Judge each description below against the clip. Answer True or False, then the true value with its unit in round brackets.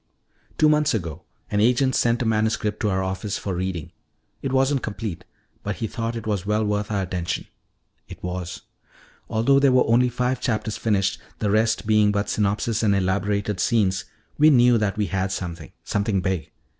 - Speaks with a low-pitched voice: True (105 Hz)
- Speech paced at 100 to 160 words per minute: False (180 wpm)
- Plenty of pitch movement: False (3.5 semitones)